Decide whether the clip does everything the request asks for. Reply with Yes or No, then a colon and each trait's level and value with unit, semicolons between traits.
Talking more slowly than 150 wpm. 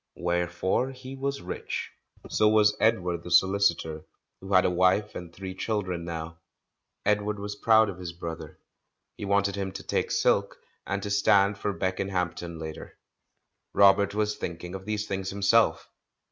No: average, 160 wpm